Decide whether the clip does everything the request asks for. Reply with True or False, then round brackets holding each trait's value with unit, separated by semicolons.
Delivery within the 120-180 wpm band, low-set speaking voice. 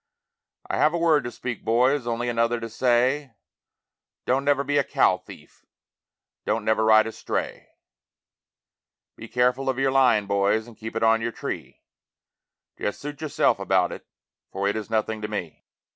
True (170 wpm; 115 Hz)